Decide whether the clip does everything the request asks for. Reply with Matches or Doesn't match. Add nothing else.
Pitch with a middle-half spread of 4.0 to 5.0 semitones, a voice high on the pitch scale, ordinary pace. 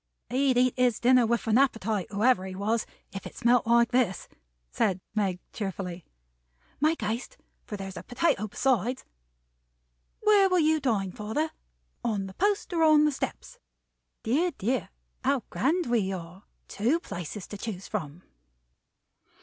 Doesn't match